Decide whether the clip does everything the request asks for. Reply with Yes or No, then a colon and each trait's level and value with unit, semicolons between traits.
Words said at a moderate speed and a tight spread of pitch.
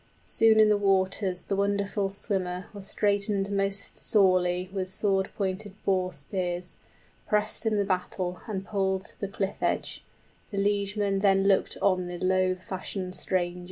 Yes: average, 160 wpm; narrow, 1.6 semitones